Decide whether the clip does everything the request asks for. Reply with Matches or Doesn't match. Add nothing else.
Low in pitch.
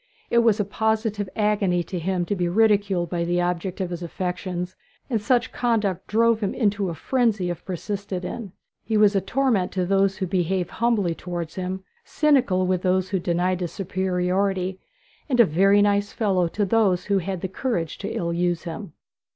Doesn't match